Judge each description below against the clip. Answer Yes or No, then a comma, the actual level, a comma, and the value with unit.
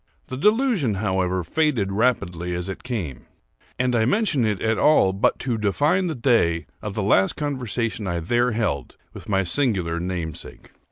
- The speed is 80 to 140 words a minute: No, average, 165 wpm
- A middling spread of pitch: No, wide, 5.7 semitones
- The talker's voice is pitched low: Yes, low, 105 Hz